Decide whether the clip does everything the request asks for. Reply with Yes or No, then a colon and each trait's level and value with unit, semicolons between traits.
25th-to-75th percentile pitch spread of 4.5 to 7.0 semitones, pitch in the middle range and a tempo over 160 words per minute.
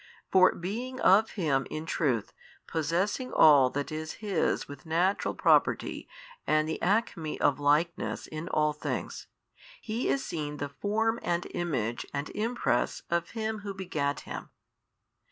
No: wide, 5.6 semitones; medium, 170 Hz; average, 140 wpm